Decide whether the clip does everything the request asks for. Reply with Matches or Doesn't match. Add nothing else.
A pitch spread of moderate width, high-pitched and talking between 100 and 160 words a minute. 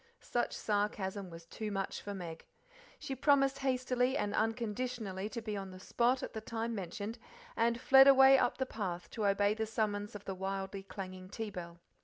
Doesn't match